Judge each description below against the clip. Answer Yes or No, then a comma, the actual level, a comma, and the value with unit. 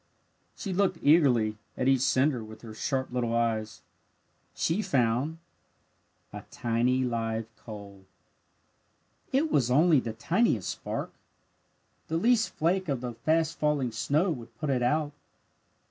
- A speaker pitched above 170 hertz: No, low, 130 Hz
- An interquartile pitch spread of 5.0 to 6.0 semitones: Yes, wide, 5.5 semitones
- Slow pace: Yes, slow, 130 wpm